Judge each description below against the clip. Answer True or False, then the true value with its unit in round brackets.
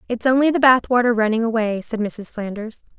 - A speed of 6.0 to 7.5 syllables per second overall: False (5.7 syllables/s)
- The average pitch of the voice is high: True (230 Hz)